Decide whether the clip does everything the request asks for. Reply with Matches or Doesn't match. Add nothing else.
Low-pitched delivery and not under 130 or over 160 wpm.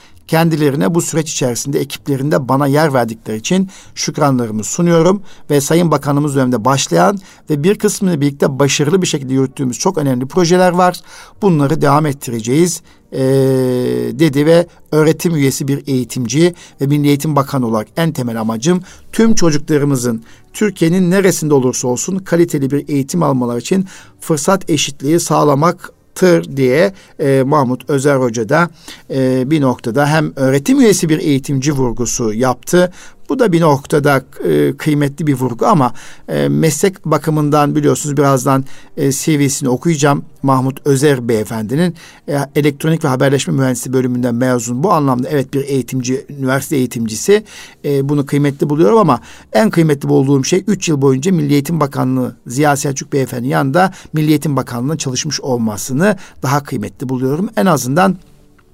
Doesn't match